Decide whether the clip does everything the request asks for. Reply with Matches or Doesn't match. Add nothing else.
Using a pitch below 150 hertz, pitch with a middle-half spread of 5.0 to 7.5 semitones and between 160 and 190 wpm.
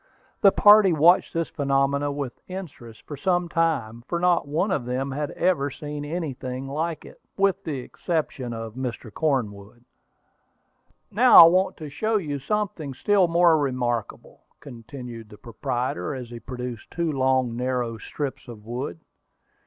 Doesn't match